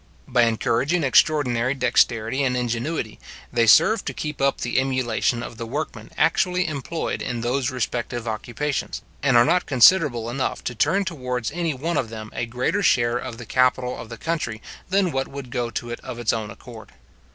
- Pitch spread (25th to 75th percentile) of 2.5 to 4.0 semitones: Yes, average, 3.5 semitones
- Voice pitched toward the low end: Yes, low, 125 Hz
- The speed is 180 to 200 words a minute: Yes, average, 185 wpm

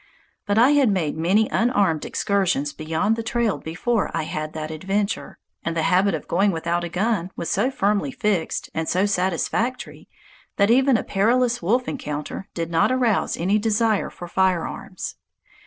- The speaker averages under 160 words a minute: No, average, 165 wpm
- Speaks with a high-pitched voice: Yes, high, 195 Hz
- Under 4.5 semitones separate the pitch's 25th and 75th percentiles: No, average, 5.1 semitones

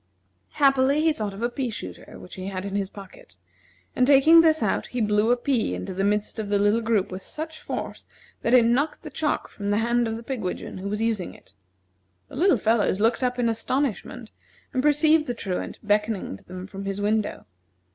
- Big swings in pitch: No, average, 4.4 semitones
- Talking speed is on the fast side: Yes, fast, 210 wpm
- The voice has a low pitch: No, high, 225 Hz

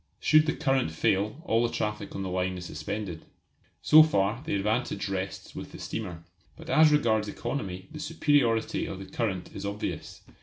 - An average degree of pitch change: No, wide, 5.9 semitones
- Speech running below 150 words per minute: No, average, 180 wpm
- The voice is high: No, low, 105 Hz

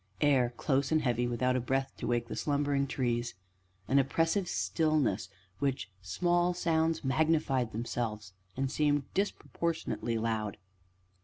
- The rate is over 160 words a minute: No, slow, 135 wpm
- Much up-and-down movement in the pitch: No, average, 4.6 semitones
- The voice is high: No, low, 135 Hz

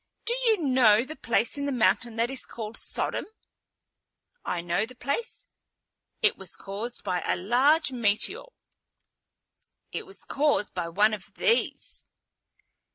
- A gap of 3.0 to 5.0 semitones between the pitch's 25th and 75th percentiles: No, wide, 5.4 semitones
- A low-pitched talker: No, high, 235 Hz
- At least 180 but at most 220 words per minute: No, average, 140 wpm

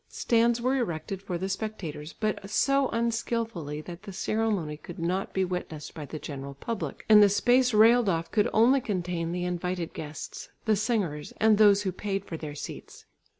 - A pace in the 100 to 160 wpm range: No, average, 180 wpm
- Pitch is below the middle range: No, high, 195 Hz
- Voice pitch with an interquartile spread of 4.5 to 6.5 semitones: Yes, average, 4.9 semitones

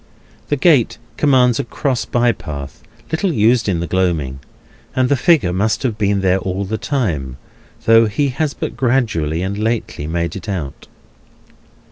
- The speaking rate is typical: Yes, average, 160 wpm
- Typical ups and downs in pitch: No, wide, 6.1 semitones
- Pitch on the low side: Yes, low, 110 Hz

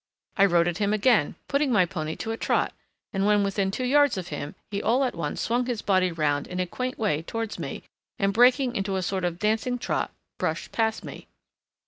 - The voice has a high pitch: Yes, high, 200 Hz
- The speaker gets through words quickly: Yes, fast, 215 wpm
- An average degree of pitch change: Yes, average, 4.8 semitones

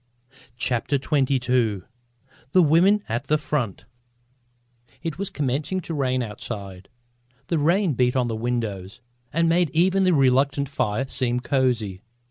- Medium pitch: No, low, 130 Hz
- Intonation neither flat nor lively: Yes, average, 4.8 semitones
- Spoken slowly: Yes, slow, 130 wpm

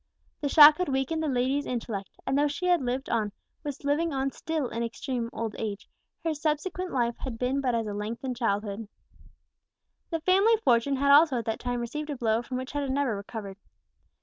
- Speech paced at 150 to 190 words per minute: No, fast, 205 wpm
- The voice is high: Yes, very high, 265 Hz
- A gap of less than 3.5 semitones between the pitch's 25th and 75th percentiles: No, average, 4.1 semitones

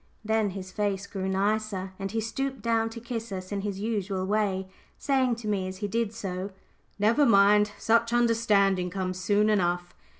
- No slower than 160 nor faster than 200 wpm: Yes, average, 180 wpm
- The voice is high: Yes, high, 205 Hz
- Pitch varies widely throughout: No, average, 2.9 semitones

